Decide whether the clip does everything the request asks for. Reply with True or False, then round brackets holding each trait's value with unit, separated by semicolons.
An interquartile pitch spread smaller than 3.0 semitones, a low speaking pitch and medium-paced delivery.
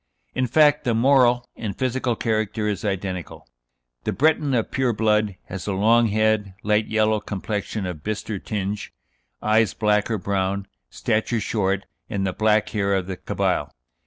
True (2.5 semitones; 105 Hz; 160 wpm)